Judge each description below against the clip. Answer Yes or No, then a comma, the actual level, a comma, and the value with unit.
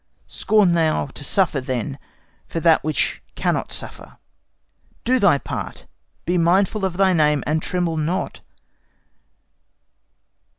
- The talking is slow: Yes, slow, 120 wpm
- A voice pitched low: No, medium, 170 Hz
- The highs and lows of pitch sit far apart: No, average, 3.9 semitones